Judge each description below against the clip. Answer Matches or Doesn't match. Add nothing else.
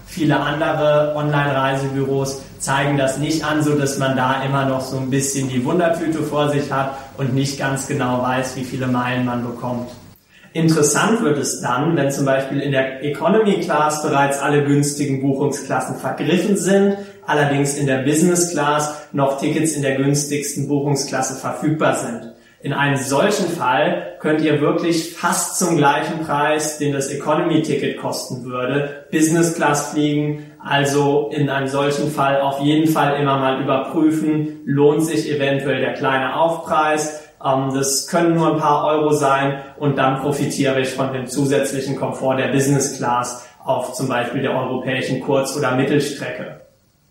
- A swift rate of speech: Doesn't match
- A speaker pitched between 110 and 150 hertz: Matches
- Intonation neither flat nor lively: Doesn't match